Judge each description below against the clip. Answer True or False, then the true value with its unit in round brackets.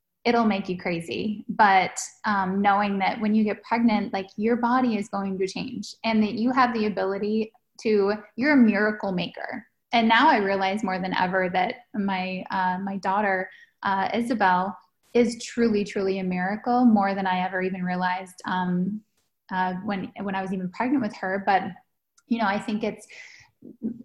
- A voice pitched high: True (205 Hz)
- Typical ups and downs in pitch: True (3.1 semitones)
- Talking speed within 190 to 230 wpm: False (175 wpm)